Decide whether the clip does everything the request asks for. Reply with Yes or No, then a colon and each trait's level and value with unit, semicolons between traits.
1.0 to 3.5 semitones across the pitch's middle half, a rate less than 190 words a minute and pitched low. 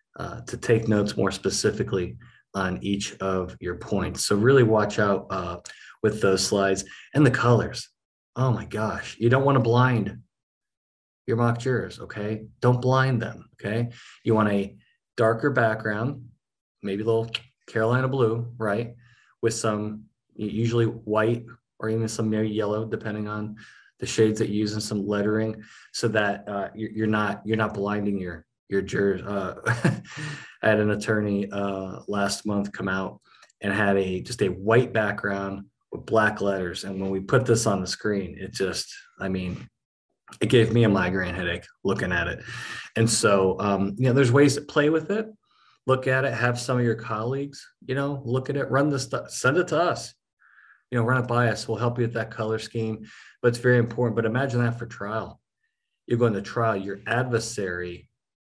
Yes: average, 3.0 semitones; average, 180 wpm; low, 110 Hz